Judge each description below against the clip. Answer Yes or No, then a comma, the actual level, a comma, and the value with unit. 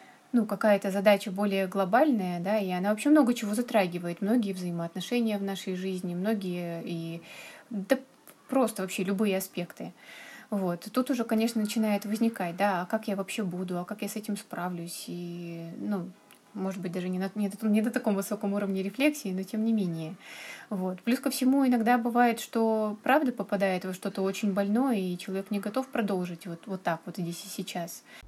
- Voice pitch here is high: Yes, high, 200 Hz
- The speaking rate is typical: No, fast, 185 wpm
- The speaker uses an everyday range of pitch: Yes, average, 3.3 semitones